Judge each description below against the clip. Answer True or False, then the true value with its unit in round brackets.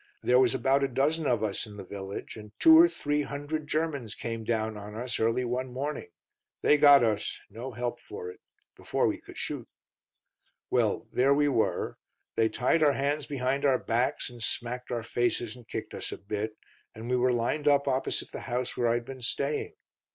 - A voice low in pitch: True (125 Hz)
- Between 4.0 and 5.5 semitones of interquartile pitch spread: False (3.5 semitones)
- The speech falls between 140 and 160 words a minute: False (195 wpm)